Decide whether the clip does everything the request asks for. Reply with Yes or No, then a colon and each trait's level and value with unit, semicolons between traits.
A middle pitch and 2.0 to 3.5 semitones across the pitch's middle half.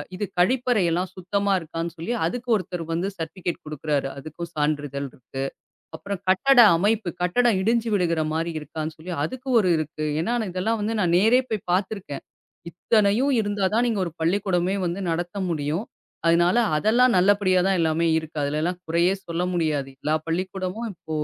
No: medium, 180 Hz; average, 4.1 semitones